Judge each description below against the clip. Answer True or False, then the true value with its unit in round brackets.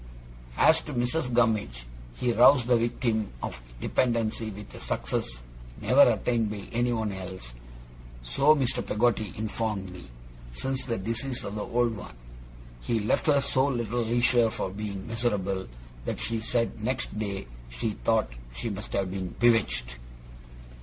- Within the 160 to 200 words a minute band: False (145 wpm)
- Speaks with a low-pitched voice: True (115 Hz)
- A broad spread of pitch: False (3.3 semitones)